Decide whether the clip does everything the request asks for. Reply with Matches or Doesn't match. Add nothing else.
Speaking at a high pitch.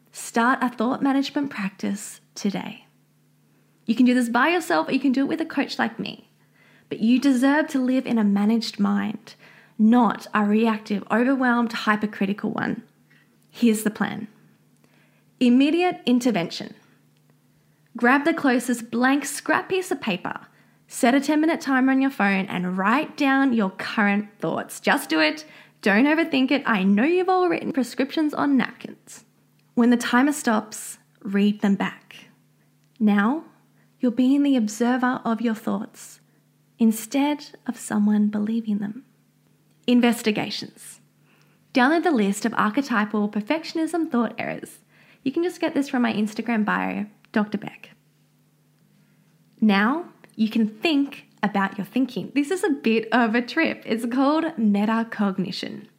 Matches